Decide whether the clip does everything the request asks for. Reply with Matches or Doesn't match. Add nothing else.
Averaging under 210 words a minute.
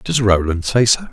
Doesn't match